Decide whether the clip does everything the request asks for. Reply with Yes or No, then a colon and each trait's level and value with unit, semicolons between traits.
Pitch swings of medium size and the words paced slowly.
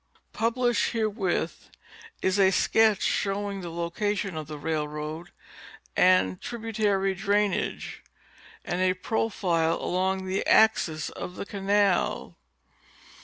Yes: average, 3.2 semitones; slow, 110 wpm